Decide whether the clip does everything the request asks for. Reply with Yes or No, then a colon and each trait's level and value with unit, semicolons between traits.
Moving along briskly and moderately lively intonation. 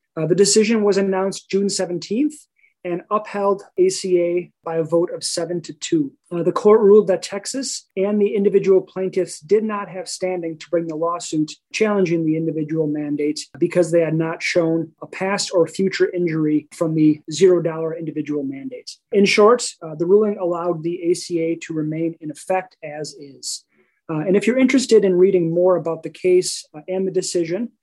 No: average, 180 wpm; average, 3.5 semitones